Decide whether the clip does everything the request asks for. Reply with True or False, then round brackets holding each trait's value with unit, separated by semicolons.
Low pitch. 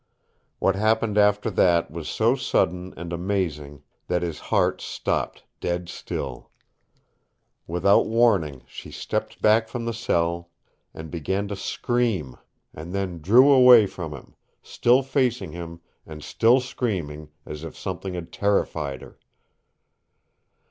True (90 Hz)